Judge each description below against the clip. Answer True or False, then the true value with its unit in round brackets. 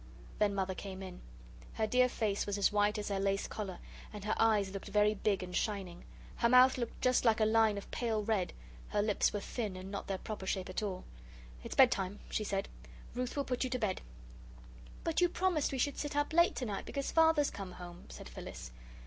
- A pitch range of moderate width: True (4.3 semitones)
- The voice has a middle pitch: False (210 Hz)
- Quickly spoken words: True (215 wpm)